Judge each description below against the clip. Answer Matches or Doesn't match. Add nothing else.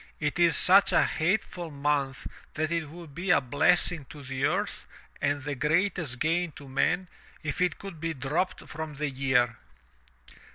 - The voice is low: Doesn't match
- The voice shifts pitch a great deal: Doesn't match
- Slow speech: Doesn't match